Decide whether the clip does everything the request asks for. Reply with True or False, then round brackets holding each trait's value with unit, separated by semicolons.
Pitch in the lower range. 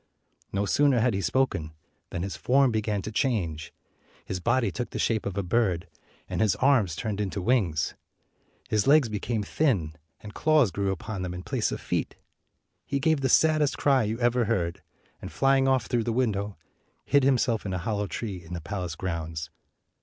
True (105 Hz)